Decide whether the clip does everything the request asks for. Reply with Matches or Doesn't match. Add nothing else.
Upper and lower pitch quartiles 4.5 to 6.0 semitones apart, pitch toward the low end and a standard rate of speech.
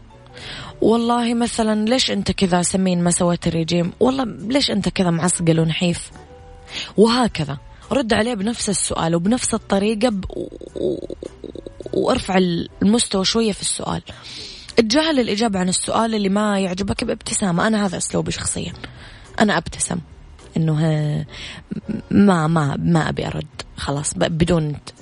Doesn't match